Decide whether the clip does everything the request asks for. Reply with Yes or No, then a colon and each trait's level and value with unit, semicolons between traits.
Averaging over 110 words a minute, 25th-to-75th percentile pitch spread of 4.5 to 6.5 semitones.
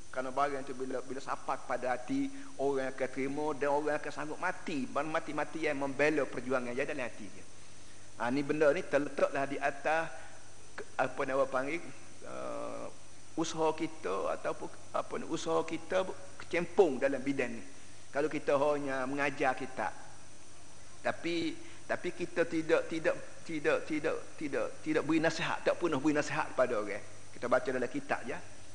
No: average, 150 wpm; average, 3.6 semitones